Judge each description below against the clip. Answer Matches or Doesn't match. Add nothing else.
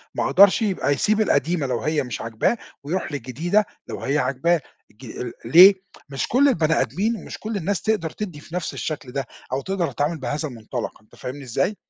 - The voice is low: Doesn't match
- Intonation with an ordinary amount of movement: Doesn't match